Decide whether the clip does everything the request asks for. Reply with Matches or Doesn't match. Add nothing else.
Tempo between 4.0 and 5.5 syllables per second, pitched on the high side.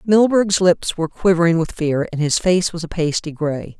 Doesn't match